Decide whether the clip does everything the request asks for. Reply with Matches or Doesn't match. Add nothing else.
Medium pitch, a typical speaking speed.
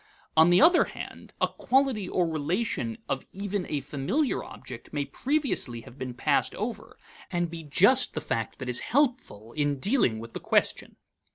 Matches